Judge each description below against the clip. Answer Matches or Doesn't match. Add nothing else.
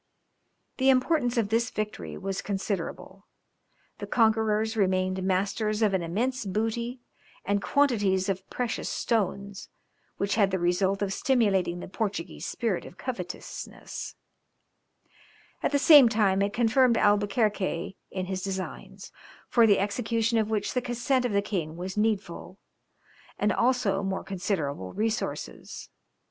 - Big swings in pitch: Doesn't match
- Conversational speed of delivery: Doesn't match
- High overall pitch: Matches